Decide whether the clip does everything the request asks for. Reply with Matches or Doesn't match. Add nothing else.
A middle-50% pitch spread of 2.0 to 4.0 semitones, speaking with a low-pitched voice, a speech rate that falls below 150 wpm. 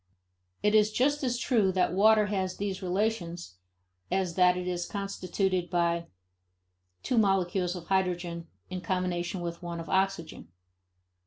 Doesn't match